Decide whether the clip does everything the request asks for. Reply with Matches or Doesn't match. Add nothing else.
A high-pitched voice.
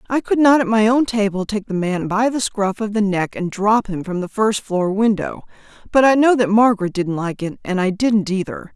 Matches